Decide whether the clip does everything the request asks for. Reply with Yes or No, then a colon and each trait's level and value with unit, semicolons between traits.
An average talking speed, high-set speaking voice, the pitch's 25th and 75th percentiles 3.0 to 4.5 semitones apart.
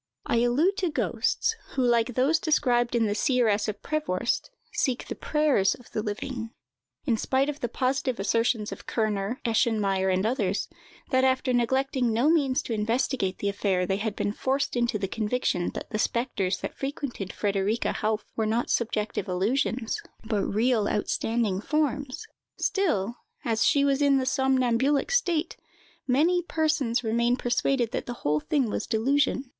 Yes: average, 160 wpm; high, 240 Hz; average, 4.1 semitones